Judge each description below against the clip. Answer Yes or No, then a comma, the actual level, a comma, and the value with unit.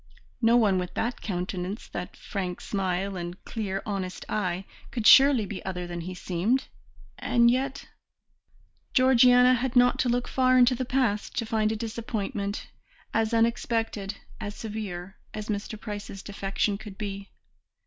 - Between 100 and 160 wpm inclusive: Yes, average, 150 wpm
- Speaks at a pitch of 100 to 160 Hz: No, high, 215 Hz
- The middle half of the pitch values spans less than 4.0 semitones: Yes, average, 3.6 semitones